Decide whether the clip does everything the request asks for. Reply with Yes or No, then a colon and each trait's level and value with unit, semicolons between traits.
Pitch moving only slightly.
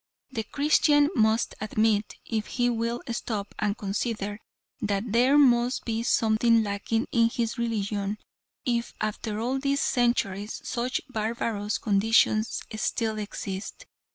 Yes: narrow, 2.2 semitones